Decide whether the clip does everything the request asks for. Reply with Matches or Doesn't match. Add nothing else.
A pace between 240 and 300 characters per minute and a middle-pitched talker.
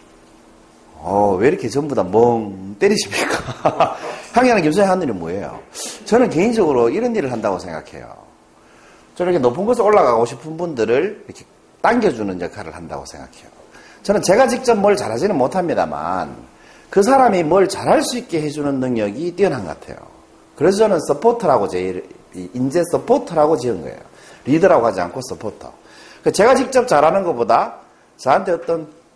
Doesn't match